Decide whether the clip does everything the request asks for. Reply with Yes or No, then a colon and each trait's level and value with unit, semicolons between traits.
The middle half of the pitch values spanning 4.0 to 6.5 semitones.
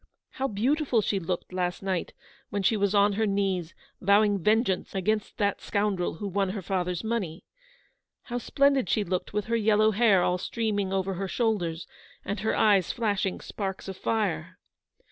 No: average, 2.7 semitones